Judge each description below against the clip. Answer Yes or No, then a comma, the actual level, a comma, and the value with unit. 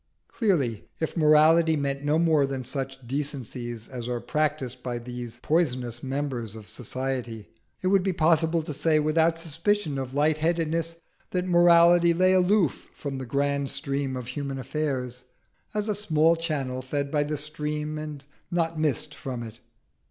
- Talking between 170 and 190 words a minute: No, average, 160 wpm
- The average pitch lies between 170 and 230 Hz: No, medium, 150 Hz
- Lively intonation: No, average, 4.0 semitones